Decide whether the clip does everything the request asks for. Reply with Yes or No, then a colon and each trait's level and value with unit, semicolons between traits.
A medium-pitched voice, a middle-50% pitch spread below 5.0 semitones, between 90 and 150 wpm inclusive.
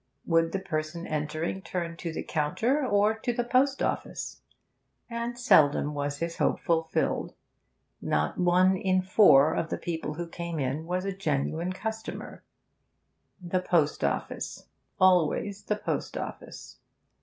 Yes: medium, 175 Hz; average, 3.9 semitones; average, 140 wpm